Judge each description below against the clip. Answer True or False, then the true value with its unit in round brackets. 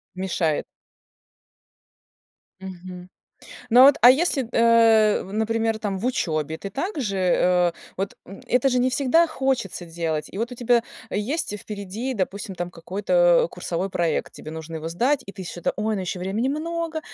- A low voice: False (210 Hz)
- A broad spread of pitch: True (5.7 semitones)